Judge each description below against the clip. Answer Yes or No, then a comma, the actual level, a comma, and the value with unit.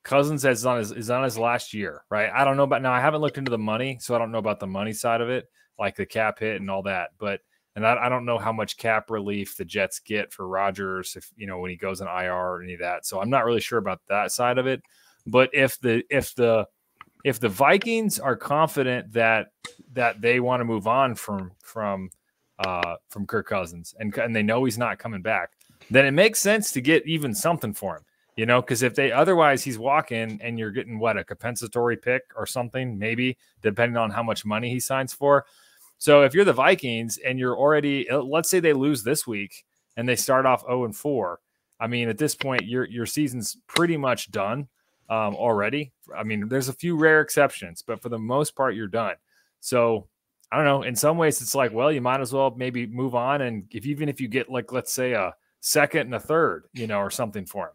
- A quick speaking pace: Yes, fast, 235 wpm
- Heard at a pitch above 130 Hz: No, low, 125 Hz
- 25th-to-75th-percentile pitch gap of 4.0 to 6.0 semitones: No, average, 3.6 semitones